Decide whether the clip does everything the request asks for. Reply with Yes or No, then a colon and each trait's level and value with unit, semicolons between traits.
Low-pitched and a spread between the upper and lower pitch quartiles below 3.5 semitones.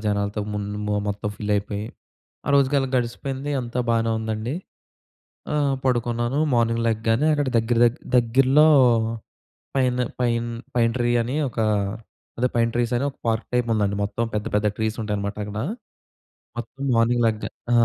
Yes: low, 115 Hz; narrow, 2.6 semitones